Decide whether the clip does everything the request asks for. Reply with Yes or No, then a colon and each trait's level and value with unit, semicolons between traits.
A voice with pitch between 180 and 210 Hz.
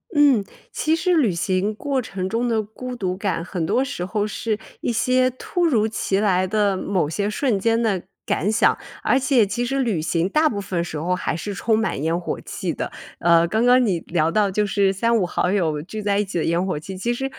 Yes: high, 205 Hz